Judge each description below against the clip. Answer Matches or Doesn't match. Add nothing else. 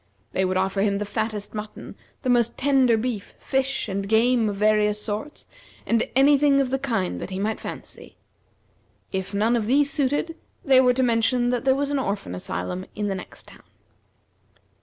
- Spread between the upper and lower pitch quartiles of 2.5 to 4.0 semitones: Doesn't match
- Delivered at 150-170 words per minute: Doesn't match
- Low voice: Doesn't match